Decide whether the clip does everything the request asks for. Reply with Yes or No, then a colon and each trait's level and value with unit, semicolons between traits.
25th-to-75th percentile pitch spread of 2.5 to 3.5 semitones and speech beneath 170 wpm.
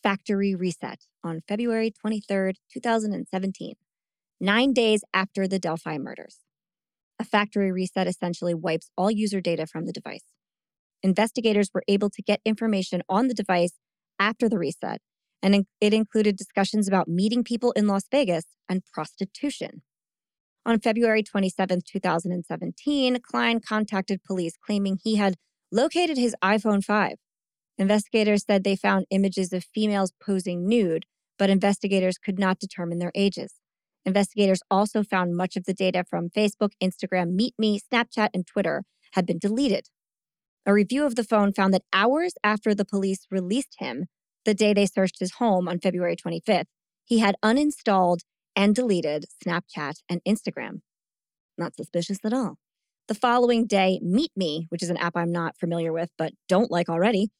Yes: average, 2.8 semitones; average, 150 wpm